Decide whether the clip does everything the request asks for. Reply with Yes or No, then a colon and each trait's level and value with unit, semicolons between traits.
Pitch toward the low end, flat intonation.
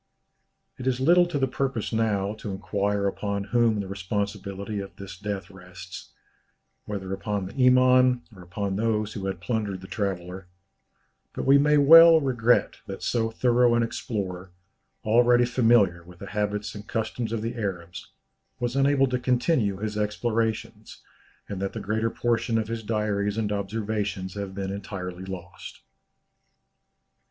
No: low, 105 Hz; average, 3.5 semitones